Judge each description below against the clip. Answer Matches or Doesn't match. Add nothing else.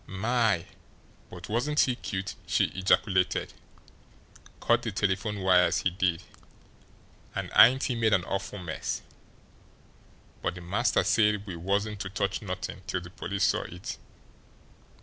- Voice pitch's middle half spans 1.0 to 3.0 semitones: Matches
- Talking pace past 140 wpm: Doesn't match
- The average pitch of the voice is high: Doesn't match